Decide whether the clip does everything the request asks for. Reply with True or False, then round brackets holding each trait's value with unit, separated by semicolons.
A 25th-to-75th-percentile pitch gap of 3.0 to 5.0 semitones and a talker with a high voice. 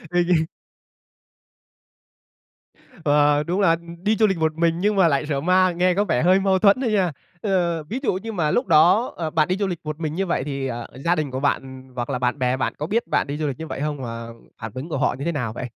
False (4.6 semitones; 165 Hz)